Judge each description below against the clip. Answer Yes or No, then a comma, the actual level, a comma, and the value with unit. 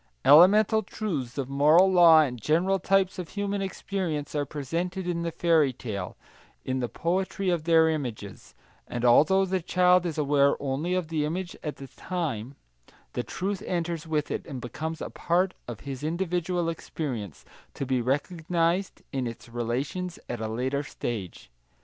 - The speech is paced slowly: No, average, 160 wpm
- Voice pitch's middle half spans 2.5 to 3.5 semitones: No, average, 5.2 semitones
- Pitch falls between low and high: Yes, medium, 160 Hz